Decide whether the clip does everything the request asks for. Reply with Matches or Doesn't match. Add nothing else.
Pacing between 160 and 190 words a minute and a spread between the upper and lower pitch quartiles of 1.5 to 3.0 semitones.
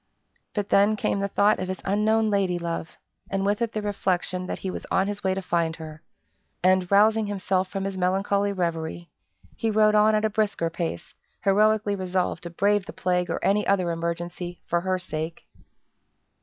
Matches